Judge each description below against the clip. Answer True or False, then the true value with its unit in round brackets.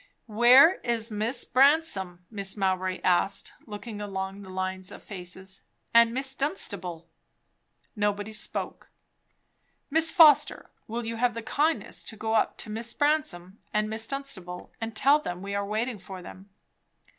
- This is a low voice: False (215 Hz)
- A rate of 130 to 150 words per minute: True (145 wpm)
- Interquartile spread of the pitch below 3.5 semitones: False (4.2 semitones)